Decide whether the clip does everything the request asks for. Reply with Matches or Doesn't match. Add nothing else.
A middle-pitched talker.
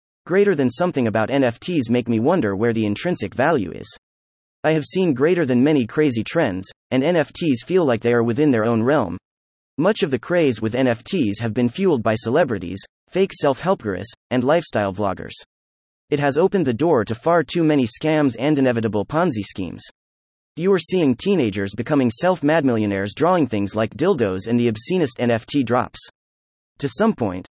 Doesn't match